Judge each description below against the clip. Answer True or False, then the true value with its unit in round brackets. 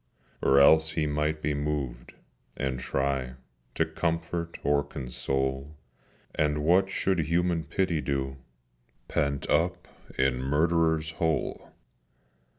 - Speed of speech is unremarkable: False (110 wpm)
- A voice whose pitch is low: True (75 Hz)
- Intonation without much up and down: False (3.3 semitones)